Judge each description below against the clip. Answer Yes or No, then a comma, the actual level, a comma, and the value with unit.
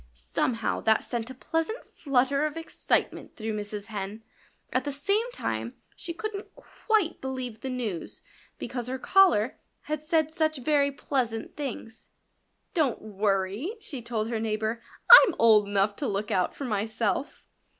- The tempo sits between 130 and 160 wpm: Yes, average, 150 wpm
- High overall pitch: Yes, high, 245 Hz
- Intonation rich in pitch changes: Yes, wide, 6.2 semitones